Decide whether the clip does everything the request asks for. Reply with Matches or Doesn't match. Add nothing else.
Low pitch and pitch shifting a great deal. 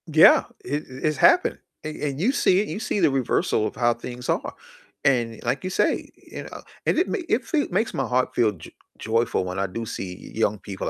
Matches